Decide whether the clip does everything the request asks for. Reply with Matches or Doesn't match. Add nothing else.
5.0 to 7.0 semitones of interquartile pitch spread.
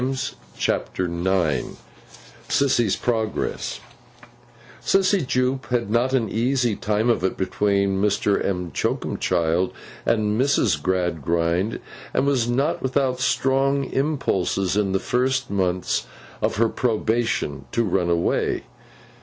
Matches